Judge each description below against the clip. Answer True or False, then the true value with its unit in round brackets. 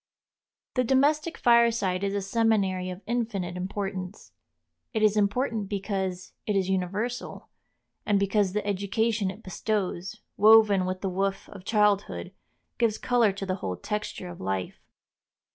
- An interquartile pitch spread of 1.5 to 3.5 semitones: True (2.8 semitones)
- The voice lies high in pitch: True (200 Hz)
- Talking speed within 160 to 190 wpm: False (140 wpm)